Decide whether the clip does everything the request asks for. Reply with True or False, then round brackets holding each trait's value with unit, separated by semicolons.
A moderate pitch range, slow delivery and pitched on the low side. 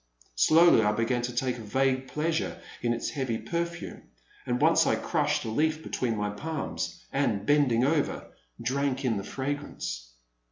False (4.2 semitones; 160 wpm; 130 Hz)